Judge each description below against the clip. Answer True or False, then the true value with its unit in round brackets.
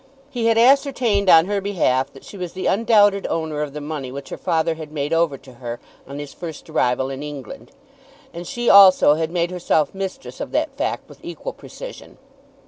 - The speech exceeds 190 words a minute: True (200 wpm)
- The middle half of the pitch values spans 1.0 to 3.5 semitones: False (5.6 semitones)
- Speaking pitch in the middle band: True (165 Hz)